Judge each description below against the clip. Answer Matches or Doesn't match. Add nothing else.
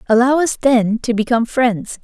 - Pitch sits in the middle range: Doesn't match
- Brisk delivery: Doesn't match